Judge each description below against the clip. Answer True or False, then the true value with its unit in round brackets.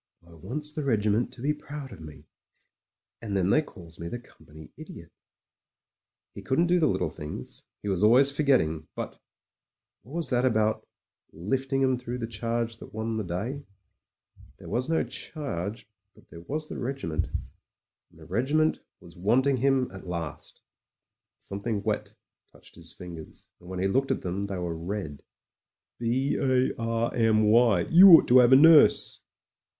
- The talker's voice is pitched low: True (115 Hz)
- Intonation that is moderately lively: False (6.6 semitones)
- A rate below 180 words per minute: False (185 wpm)